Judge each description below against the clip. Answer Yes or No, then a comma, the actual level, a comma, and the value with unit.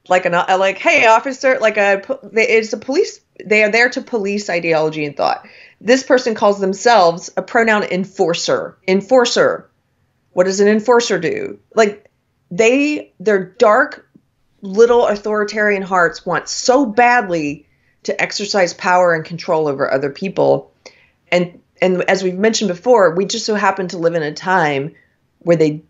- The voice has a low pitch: No, high, 195 Hz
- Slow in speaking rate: No, average, 155 wpm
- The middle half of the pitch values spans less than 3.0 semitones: No, average, 4.6 semitones